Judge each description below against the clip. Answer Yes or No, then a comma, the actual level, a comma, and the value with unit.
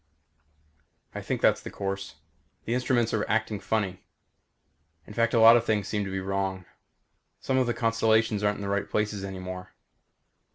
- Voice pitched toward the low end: Yes, low, 105 Hz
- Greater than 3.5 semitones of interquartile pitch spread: No, average, 2.7 semitones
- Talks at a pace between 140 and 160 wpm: No, average, 170 wpm